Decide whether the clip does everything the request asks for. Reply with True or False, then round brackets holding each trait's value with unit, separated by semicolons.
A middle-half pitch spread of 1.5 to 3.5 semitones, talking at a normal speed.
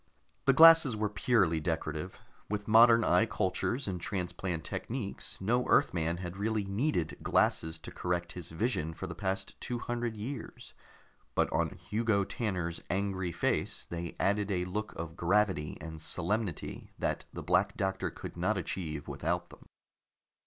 False (4.3 semitones; 150 wpm)